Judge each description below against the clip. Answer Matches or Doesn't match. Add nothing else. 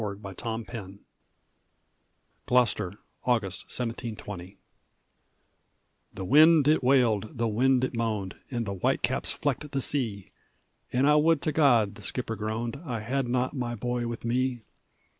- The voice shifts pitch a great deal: Doesn't match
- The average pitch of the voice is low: Matches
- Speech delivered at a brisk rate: Doesn't match